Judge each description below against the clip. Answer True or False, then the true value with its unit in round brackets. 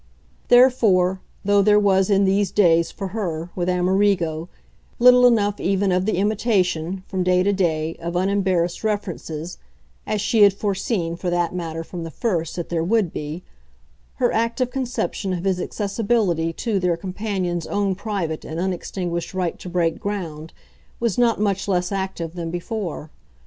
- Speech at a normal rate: True (160 wpm)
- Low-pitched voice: False (185 Hz)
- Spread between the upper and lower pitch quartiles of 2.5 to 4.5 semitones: True (3.1 semitones)